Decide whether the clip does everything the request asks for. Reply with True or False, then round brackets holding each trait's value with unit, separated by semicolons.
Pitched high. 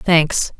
False (165 Hz)